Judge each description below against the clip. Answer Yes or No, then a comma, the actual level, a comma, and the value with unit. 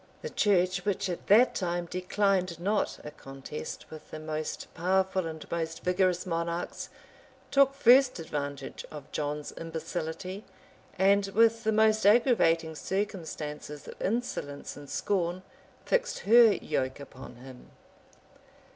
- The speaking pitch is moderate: Yes, medium, 180 Hz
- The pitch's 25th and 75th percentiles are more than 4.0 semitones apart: Yes, average, 4.6 semitones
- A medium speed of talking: No, slow, 125 wpm